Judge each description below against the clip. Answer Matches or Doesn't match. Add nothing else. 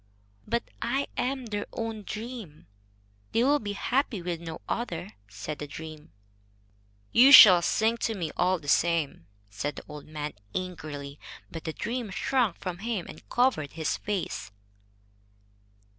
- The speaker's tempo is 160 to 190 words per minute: Doesn't match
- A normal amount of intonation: Doesn't match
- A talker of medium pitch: Matches